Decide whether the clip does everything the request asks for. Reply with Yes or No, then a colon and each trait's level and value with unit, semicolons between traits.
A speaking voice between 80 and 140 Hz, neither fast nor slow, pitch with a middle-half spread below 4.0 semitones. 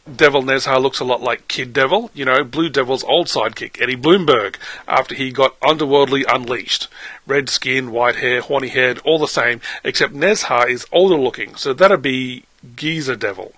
Yes: low, 135 Hz; average, 175 wpm; average, 3.6 semitones